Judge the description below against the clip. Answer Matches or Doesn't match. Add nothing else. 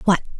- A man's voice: Doesn't match